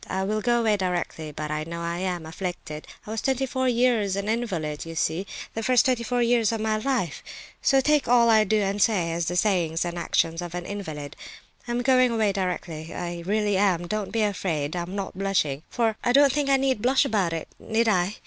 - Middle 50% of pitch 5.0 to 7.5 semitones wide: Yes, average, 5.3 semitones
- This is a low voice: No, high, 200 Hz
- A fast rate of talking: Yes, fast, 215 wpm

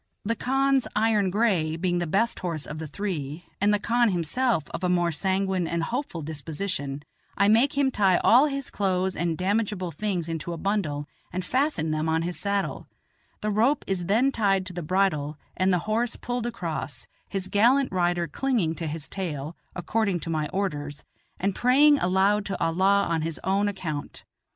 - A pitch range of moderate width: Yes, average, 4.4 semitones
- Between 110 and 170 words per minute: No, average, 180 wpm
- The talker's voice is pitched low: No, high, 190 Hz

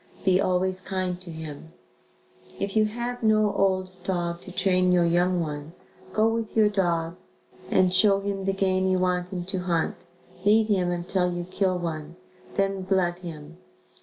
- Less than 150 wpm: No, average, 165 wpm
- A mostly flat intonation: Yes, narrow, 2.0 semitones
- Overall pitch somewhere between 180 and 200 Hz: Yes, medium, 185 Hz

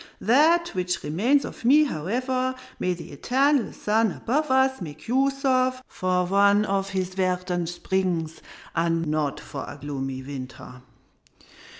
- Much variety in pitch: Yes, wide, 7.6 semitones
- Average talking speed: No, slow, 130 wpm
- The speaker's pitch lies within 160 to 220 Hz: Yes, high, 190 Hz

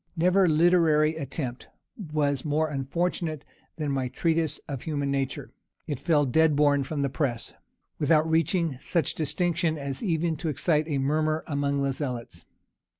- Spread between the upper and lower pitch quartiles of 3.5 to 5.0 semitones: No, narrow, 2.6 semitones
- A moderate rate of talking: Yes, average, 150 wpm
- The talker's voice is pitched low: No, medium, 150 Hz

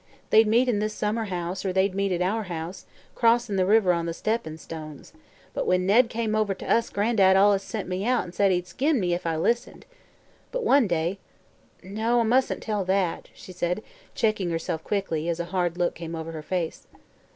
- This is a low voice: No, high, 190 Hz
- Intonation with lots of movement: No, average, 4.0 semitones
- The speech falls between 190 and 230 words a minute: Yes, fast, 205 wpm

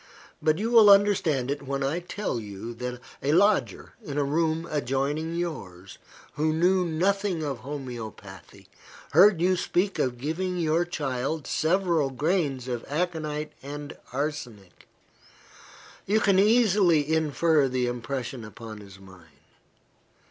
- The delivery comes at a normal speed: No, slow, 130 wpm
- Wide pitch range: Yes, wide, 5.7 semitones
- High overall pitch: No, medium, 150 Hz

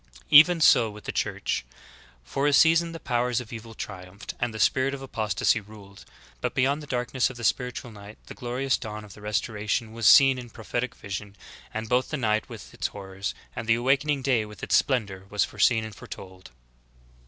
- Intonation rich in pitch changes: No, average, 3.7 semitones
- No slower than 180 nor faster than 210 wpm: Yes, average, 200 wpm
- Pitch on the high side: No, low, 115 Hz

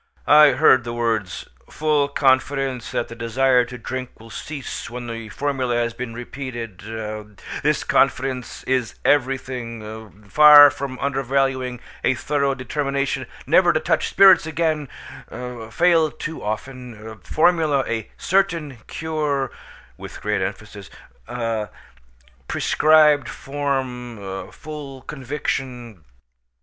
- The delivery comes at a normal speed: No, slow, 110 wpm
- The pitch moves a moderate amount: Yes, average, 3.5 semitones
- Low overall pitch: Yes, low, 130 Hz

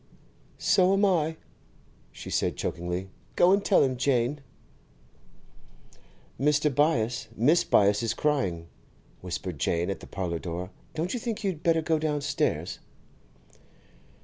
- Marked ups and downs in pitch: Yes, wide, 9.0 semitones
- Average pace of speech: No, slow, 125 wpm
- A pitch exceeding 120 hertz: Yes, medium, 140 Hz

